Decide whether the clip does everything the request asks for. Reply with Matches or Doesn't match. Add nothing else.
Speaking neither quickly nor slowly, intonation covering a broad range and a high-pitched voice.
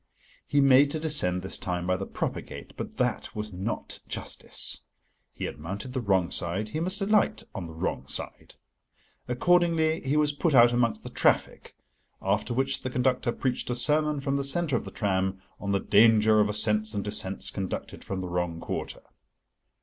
Doesn't match